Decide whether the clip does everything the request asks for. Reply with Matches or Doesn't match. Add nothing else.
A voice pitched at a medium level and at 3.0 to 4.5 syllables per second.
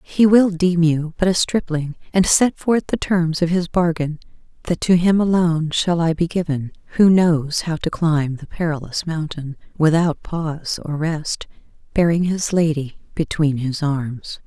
Matches